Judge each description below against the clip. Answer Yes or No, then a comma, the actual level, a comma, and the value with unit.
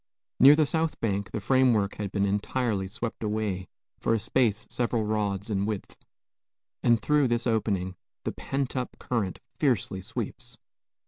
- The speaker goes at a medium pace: Yes, average, 150 wpm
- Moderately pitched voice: No, low, 110 Hz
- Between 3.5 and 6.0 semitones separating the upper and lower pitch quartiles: Yes, average, 3.8 semitones